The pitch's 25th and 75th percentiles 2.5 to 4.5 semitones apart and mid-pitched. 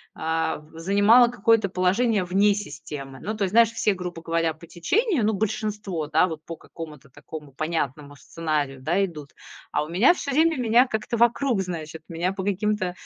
No: average, 5.2 semitones; medium, 180 Hz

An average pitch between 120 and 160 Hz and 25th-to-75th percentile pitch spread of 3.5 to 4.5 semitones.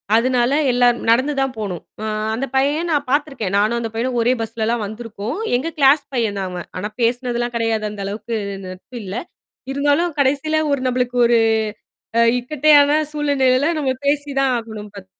No: high, 245 Hz; average, 3.9 semitones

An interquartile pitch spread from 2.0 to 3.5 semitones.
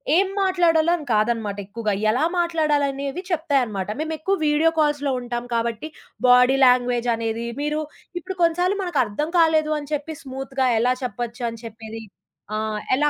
No: average, 5.2 semitones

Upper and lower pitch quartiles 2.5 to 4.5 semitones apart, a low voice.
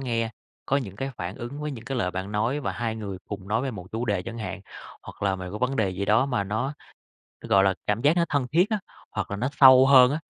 No: average, 5.1 semitones; low, 115 Hz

